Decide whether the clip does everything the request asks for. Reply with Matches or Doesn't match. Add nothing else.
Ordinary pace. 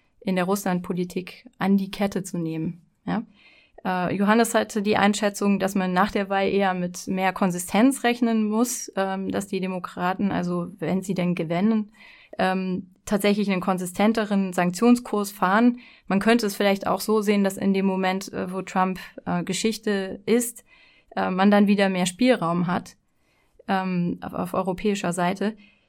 Matches